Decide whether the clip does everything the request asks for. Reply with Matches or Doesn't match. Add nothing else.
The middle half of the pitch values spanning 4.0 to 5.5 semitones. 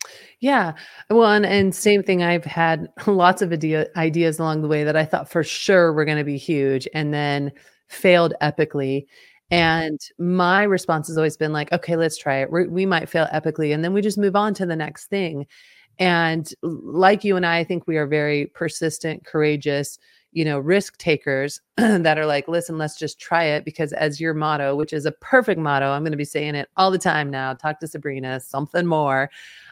Doesn't match